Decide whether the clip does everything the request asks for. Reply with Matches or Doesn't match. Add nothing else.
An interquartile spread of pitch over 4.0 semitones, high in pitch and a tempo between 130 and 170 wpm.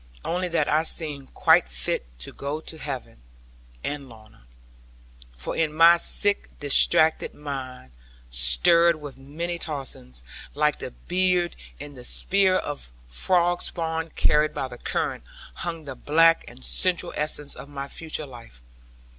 Doesn't match